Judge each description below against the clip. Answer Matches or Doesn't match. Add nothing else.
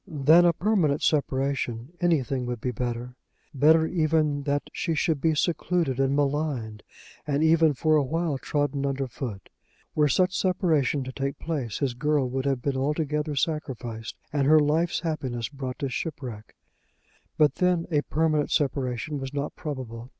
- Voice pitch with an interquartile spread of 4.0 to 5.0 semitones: Doesn't match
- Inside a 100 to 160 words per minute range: Matches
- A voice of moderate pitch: Matches